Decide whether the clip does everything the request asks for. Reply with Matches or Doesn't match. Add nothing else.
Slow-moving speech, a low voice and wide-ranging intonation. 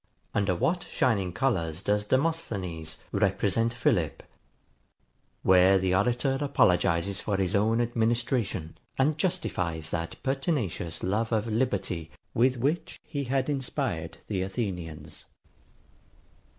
Matches